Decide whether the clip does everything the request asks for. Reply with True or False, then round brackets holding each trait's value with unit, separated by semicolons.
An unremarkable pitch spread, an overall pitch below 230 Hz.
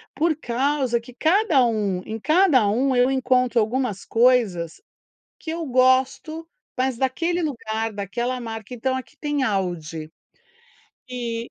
False (3.3 semitones; 250 Hz)